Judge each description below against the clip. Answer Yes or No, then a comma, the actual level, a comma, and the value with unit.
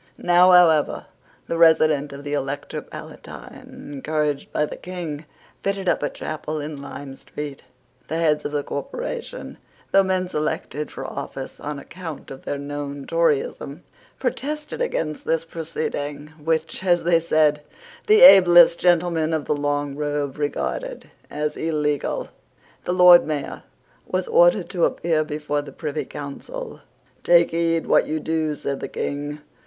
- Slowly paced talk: No, average, 145 wpm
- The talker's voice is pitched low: No, medium, 155 Hz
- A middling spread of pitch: Yes, average, 3.0 semitones